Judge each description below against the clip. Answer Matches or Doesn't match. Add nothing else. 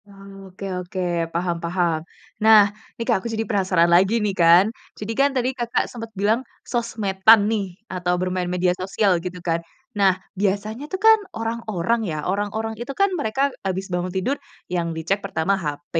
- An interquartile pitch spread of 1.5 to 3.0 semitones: Doesn't match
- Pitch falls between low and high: Doesn't match